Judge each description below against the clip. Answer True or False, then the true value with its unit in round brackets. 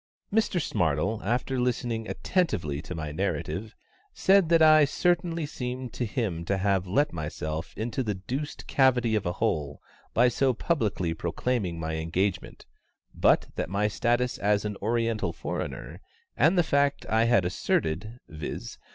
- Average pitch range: False (6.7 semitones)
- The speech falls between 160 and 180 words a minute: False (150 wpm)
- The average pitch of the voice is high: False (110 Hz)